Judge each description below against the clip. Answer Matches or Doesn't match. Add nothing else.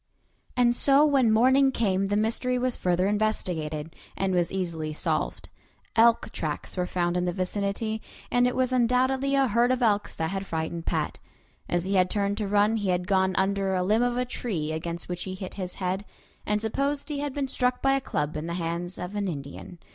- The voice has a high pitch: Matches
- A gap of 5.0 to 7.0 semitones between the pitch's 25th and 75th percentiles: Matches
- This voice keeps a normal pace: Doesn't match